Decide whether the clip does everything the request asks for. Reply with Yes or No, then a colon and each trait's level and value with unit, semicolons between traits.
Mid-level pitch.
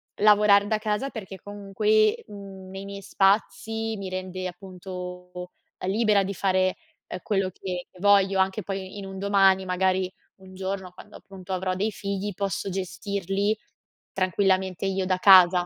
No: high, 195 Hz